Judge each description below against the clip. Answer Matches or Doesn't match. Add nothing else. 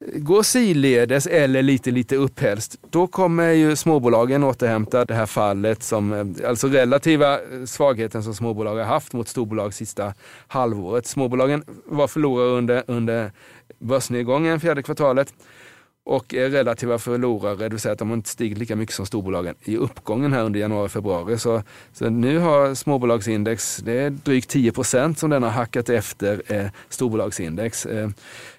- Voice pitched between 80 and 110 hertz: Doesn't match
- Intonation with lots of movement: Doesn't match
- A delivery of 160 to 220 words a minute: Doesn't match